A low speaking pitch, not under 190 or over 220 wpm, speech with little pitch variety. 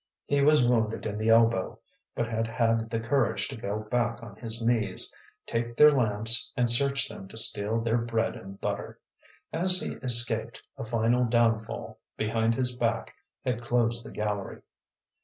No: low, 115 Hz; average, 165 wpm; narrow, 1.4 semitones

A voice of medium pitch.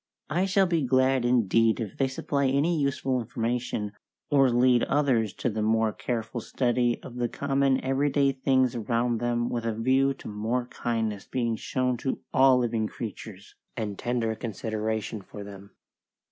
No: low, 120 Hz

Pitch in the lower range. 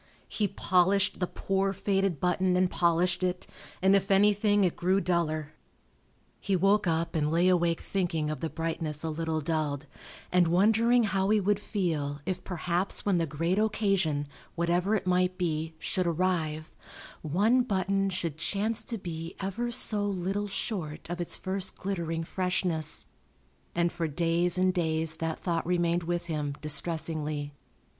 No: medium, 175 Hz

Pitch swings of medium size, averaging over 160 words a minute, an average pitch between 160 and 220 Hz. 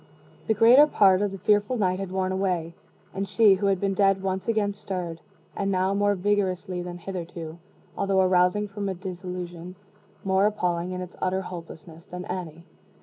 No: narrow, 1.8 semitones; average, 175 wpm; high, 190 Hz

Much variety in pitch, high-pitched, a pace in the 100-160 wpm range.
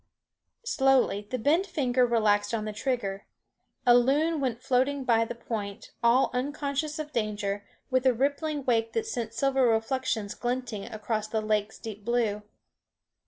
No: average, 3.8 semitones; high, 240 Hz; average, 150 wpm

